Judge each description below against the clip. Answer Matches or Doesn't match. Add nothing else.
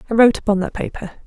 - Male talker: Doesn't match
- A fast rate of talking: Matches